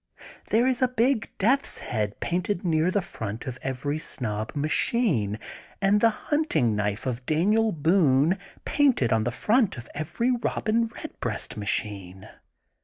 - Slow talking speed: No, average, 145 wpm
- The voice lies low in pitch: No, medium, 160 Hz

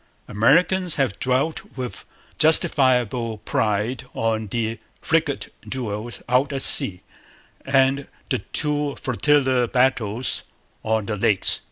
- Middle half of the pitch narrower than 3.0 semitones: No, average, 3.9 semitones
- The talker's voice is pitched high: No, low, 125 Hz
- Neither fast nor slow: No, slow, 110 wpm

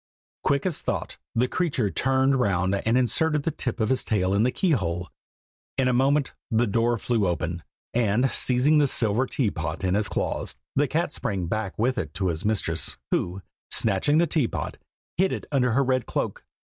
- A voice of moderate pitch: No, low, 120 Hz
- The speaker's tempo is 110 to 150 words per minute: No, average, 190 wpm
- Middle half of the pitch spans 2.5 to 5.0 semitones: No, wide, 5.4 semitones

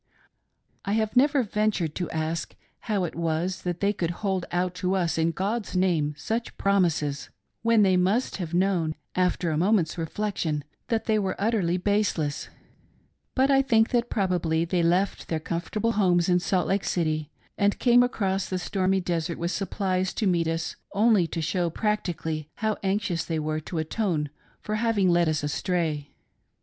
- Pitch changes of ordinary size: Yes, average, 3.9 semitones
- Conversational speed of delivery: Yes, average, 170 wpm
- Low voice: No, medium, 185 Hz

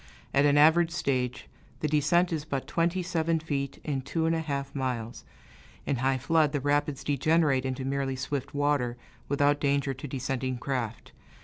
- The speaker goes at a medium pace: Yes, average, 170 wpm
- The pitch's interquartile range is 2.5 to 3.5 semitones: Yes, average, 2.8 semitones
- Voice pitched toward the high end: No, medium, 140 Hz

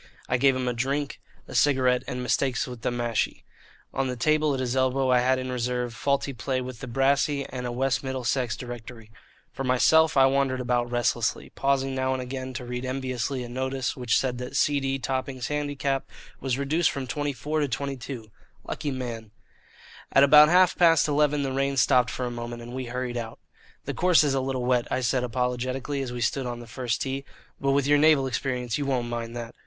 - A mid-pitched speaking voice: No, low, 130 Hz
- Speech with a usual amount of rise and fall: No, narrow, 2.0 semitones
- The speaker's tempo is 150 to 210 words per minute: Yes, fast, 205 wpm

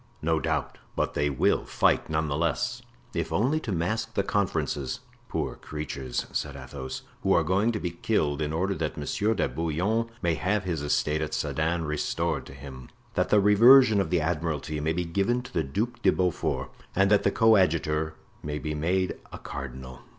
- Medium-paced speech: Yes, average, 185 wpm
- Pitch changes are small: No, average, 5.2 semitones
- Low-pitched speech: Yes, very low, 80 Hz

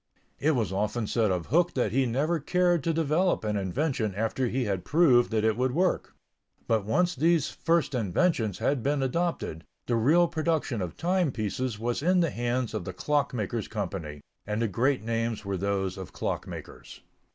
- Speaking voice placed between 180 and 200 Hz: No, low, 120 Hz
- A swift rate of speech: No, average, 185 wpm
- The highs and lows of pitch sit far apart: Yes, wide, 6.7 semitones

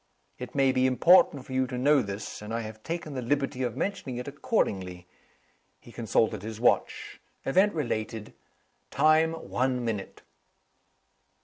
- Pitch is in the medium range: No, low, 125 Hz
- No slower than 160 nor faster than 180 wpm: No, average, 145 wpm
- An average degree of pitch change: Yes, average, 4.4 semitones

